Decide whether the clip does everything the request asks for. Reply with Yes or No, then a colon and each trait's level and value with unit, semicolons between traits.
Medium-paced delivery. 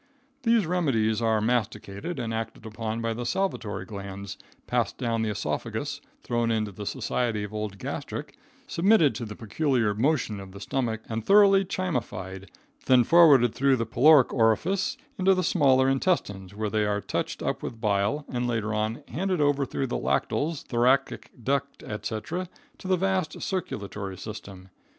Yes: average, 160 wpm